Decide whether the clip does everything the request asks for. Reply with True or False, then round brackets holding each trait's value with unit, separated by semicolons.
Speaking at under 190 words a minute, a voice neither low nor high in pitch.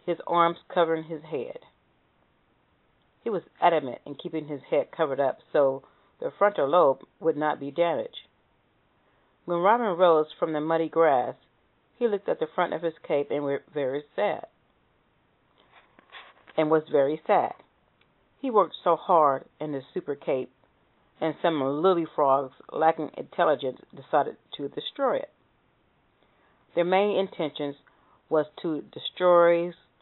True (140 wpm; 165 Hz)